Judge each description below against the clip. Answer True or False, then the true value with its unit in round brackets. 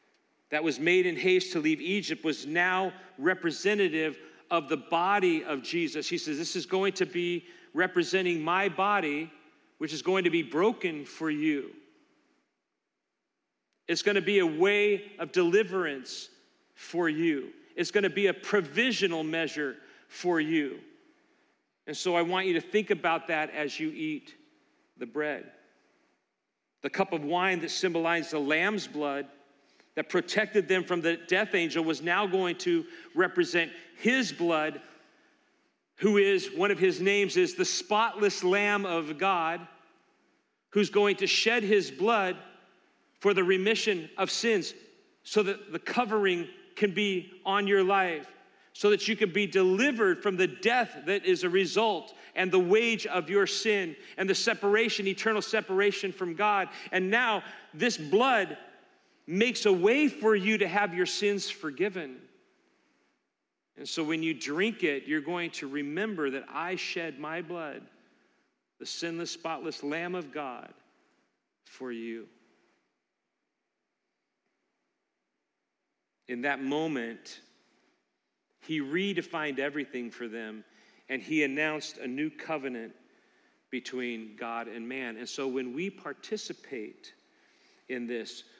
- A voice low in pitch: False (190 Hz)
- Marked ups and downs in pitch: True (5.8 semitones)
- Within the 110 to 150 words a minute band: True (140 wpm)